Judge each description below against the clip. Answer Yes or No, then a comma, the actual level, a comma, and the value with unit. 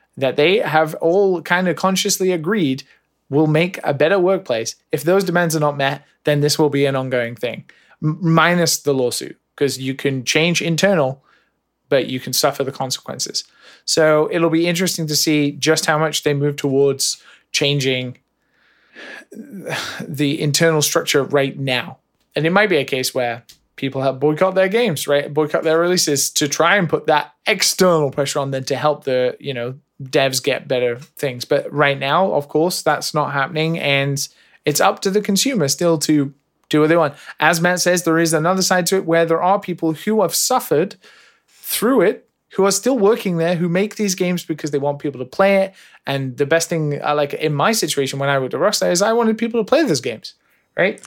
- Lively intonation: No, average, 4.1 semitones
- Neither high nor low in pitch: Yes, medium, 155 Hz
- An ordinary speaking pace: Yes, average, 195 wpm